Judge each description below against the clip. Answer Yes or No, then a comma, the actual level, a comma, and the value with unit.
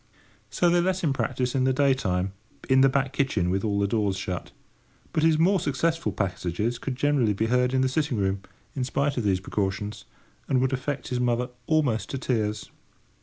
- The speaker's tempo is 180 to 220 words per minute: Yes, average, 200 wpm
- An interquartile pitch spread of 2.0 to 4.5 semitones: No, average, 5.1 semitones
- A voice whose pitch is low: Yes, low, 125 Hz